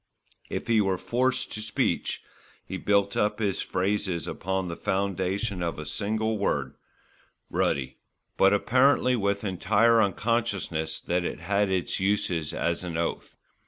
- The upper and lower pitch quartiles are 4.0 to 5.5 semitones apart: No, average, 3.1 semitones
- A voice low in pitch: Yes, low, 100 Hz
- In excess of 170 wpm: No, average, 140 wpm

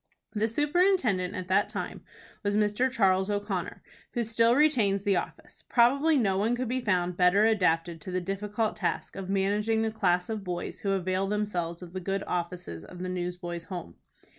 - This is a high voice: Yes, high, 195 Hz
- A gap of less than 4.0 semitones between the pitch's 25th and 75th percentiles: Yes, average, 3.5 semitones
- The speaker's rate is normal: Yes, average, 180 wpm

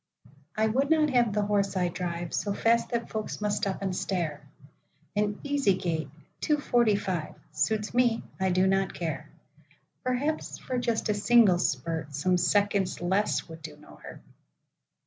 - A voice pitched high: Yes, high, 200 Hz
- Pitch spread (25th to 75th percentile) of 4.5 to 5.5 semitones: Yes, average, 4.8 semitones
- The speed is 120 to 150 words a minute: Yes, average, 140 wpm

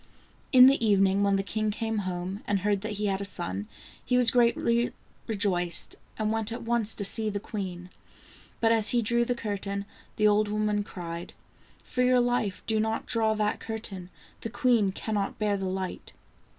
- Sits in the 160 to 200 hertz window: No, high, 210 Hz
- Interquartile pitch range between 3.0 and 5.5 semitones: No, narrow, 2.5 semitones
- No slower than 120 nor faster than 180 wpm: No, average, 190 wpm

